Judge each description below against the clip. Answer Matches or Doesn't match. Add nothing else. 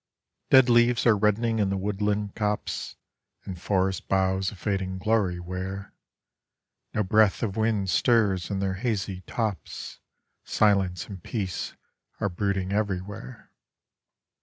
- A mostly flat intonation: Matches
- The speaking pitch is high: Doesn't match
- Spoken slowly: Matches